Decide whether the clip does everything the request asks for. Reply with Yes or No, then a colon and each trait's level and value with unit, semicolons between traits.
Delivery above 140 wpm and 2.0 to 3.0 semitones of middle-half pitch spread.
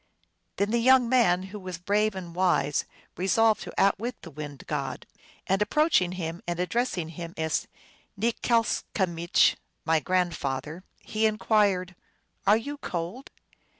No: average, 150 wpm; average, 4.3 semitones